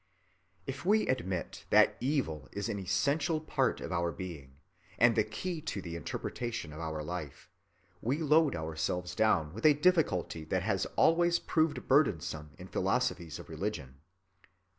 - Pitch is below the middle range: Yes, low, 105 Hz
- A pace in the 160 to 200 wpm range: No, average, 150 wpm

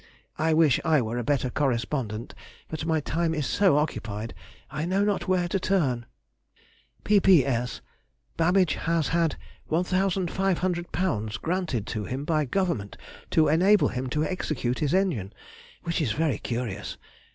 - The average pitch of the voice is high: No, medium, 155 Hz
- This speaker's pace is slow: Yes, slow, 130 wpm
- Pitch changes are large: Yes, wide, 6.5 semitones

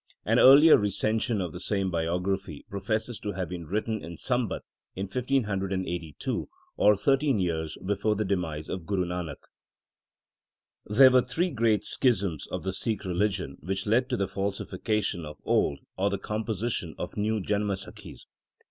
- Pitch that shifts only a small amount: No, average, 3.5 semitones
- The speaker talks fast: No, average, 150 wpm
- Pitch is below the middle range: Yes, low, 100 Hz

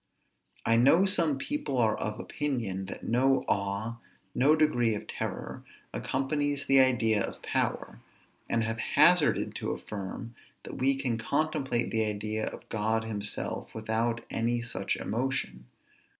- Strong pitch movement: No, average, 3.8 semitones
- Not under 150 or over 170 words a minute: No, slow, 135 wpm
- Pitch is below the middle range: Yes, low, 120 Hz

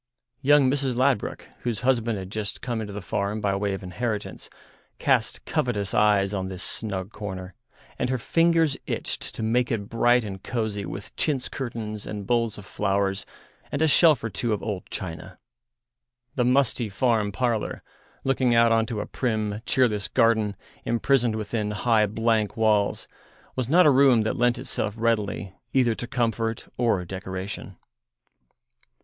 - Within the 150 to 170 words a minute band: Yes, average, 160 wpm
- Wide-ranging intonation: No, average, 3.2 semitones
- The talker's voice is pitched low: Yes, low, 110 Hz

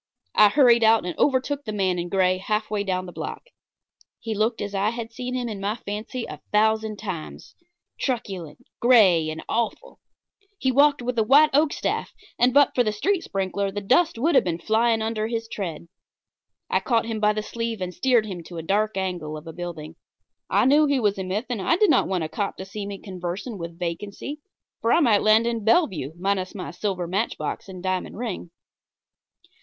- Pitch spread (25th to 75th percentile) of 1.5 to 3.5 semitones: No, average, 4.1 semitones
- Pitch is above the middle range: Yes, high, 210 Hz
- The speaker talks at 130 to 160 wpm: No, fast, 205 wpm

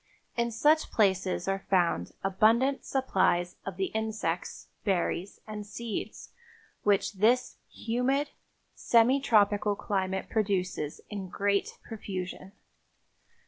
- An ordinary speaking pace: No, slow, 100 wpm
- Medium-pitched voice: No, high, 205 Hz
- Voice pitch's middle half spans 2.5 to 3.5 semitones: Yes, average, 3.2 semitones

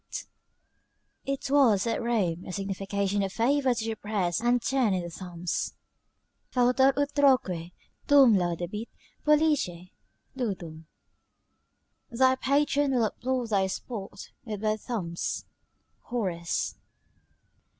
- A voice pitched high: Yes, high, 220 Hz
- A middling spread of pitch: No, wide, 5.8 semitones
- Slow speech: Yes, slow, 110 wpm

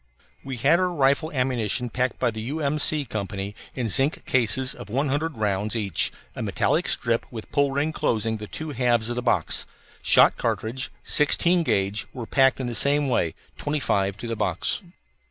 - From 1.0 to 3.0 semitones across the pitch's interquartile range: No, average, 4.4 semitones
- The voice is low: Yes, low, 125 Hz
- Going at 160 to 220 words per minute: Yes, average, 185 wpm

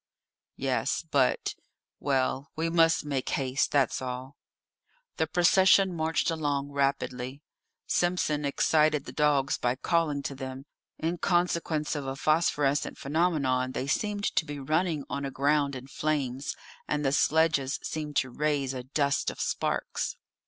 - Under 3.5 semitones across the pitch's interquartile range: Yes, average, 2.8 semitones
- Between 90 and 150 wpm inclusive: Yes, average, 140 wpm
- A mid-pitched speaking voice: Yes, medium, 145 Hz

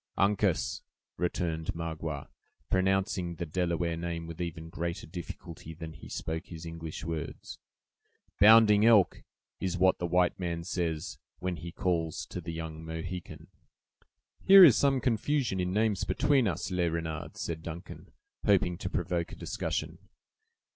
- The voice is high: No, very low, 85 Hz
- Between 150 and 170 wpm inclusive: No, average, 140 wpm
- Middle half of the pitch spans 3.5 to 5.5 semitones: No, narrow, 2.5 semitones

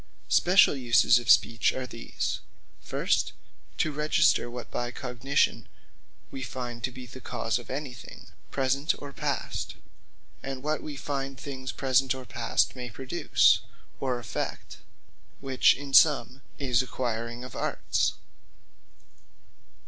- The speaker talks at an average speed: No, slow, 130 wpm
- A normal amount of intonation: No, narrow, 2.1 semitones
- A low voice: Yes, low, 130 Hz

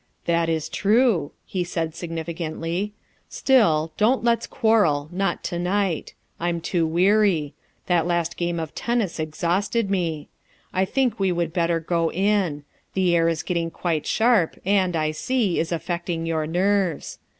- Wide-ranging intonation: No, average, 3.3 semitones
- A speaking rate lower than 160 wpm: Yes, average, 150 wpm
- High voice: No, medium, 175 Hz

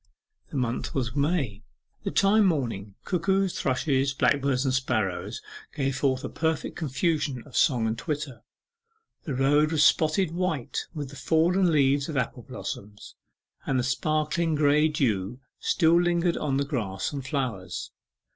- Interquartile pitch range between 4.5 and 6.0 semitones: No, average, 4.0 semitones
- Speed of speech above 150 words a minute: No, average, 145 wpm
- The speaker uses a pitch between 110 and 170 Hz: Yes, medium, 140 Hz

